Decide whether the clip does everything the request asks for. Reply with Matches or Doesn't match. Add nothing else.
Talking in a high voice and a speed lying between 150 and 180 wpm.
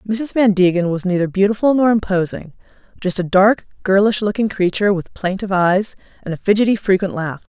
Matches